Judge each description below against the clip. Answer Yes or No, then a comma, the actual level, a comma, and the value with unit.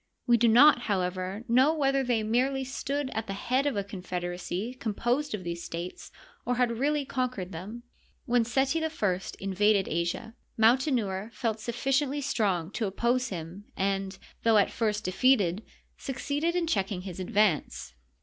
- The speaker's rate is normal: Yes, average, 150 wpm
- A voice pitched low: No, high, 225 Hz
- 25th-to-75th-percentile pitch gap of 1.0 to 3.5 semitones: No, average, 5.2 semitones